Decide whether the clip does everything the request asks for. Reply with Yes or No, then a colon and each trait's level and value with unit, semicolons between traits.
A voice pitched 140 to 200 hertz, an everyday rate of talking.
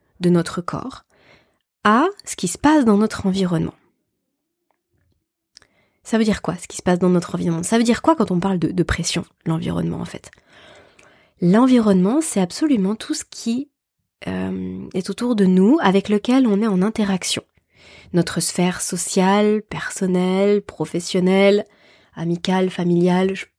Yes: high, 190 Hz; average, 155 wpm